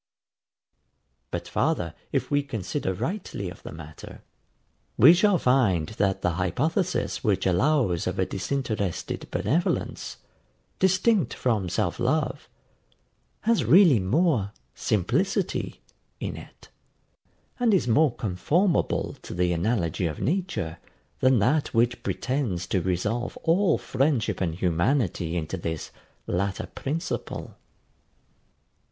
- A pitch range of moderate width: No, wide, 8.9 semitones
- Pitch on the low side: Yes, low, 115 Hz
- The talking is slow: Yes, slow, 110 wpm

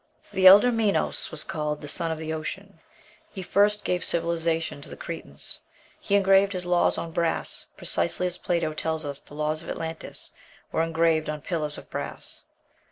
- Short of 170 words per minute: No, average, 175 wpm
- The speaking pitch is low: No, medium, 165 Hz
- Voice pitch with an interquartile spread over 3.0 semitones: No, average, 2.7 semitones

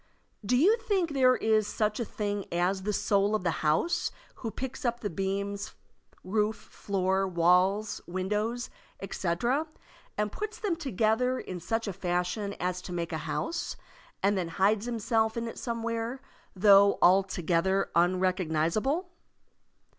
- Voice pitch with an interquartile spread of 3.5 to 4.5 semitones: Yes, average, 4.0 semitones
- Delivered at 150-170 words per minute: No, average, 140 wpm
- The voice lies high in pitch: Yes, high, 205 Hz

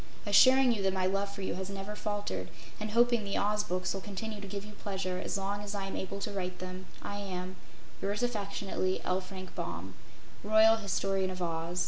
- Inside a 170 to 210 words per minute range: Yes, fast, 205 wpm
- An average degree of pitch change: No, narrow, 2.0 semitones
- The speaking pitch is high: Yes, high, 195 Hz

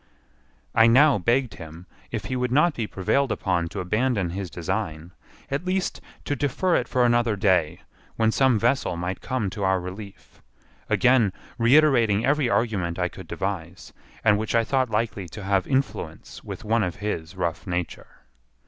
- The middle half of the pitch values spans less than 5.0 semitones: No, wide, 5.5 semitones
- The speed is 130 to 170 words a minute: Yes, average, 165 wpm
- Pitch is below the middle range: Yes, low, 105 Hz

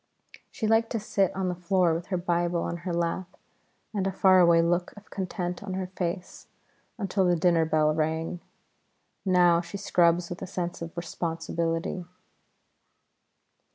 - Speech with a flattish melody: Yes, narrow, 1.8 semitones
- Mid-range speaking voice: Yes, medium, 175 Hz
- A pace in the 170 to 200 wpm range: No, average, 155 wpm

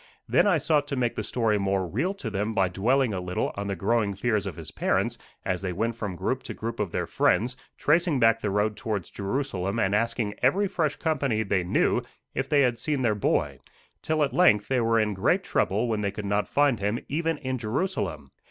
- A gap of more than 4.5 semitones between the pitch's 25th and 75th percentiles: Yes, average, 5.3 semitones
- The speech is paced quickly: Yes, fast, 220 wpm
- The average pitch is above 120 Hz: No, low, 115 Hz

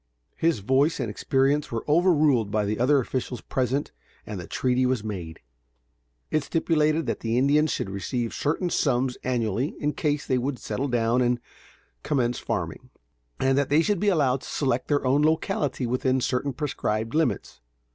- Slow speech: No, average, 165 wpm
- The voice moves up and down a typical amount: Yes, average, 3.6 semitones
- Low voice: Yes, low, 130 Hz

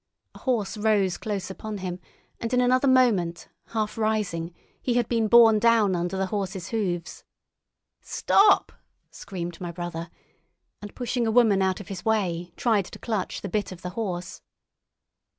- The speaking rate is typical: Yes, average, 160 wpm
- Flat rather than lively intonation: No, average, 3.9 semitones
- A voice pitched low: No, high, 205 Hz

